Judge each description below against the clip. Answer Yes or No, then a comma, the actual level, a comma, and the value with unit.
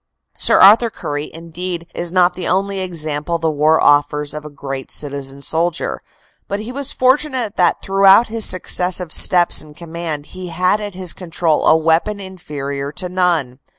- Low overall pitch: No, medium, 175 Hz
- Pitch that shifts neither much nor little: Yes, average, 3.8 semitones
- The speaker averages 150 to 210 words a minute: Yes, average, 170 wpm